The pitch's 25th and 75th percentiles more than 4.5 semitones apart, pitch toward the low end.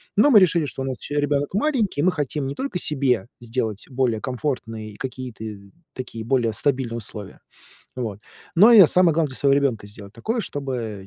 Yes: average, 5.1 semitones; low, 130 Hz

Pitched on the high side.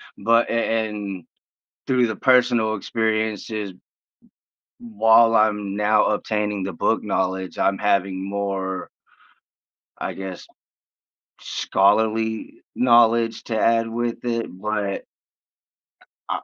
No: low, 110 Hz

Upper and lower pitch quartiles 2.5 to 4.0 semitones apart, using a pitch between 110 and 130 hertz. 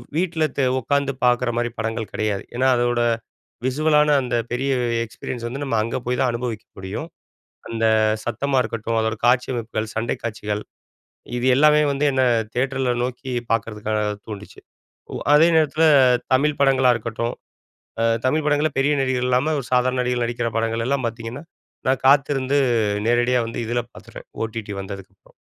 Yes: average, 3.0 semitones; low, 125 Hz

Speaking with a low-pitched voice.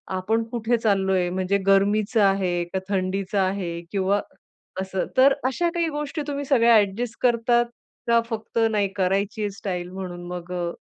No: high, 200 Hz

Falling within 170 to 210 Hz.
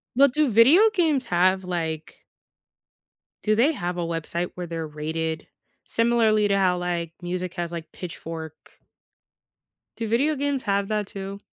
Yes: medium, 185 Hz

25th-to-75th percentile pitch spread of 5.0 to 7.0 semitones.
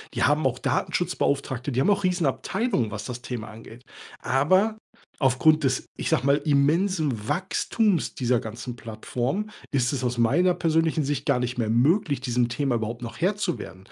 Yes: wide, 5.4 semitones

